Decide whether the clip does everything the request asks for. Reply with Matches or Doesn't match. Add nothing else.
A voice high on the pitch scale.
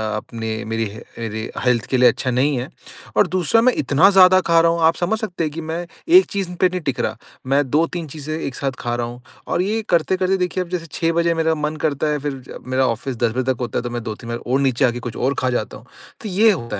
Doesn't match